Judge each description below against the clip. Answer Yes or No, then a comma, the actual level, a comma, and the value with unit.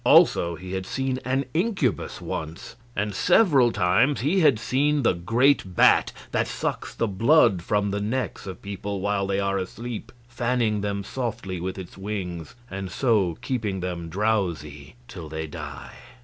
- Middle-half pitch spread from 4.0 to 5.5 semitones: Yes, average, 5.0 semitones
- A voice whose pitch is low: Yes, low, 100 Hz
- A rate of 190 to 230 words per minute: No, average, 160 wpm